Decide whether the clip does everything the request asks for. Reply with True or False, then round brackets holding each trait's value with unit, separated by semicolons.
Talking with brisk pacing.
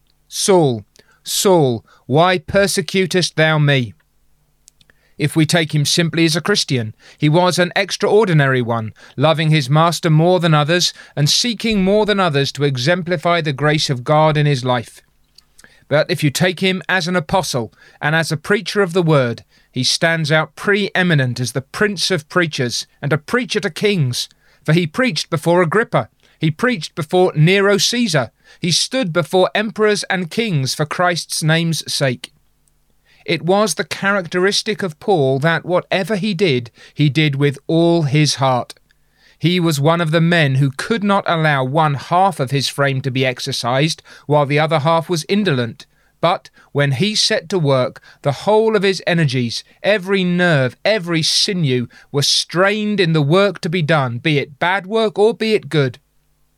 False (170 wpm)